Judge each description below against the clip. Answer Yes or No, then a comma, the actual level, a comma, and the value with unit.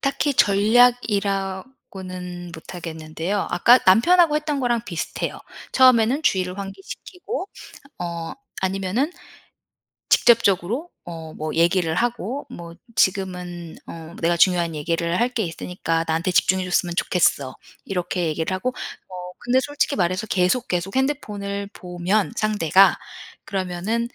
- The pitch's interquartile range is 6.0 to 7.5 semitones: No, average, 5.1 semitones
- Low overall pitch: No, high, 190 Hz